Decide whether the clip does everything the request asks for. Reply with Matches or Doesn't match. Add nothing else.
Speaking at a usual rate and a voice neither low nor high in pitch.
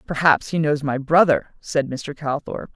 Matches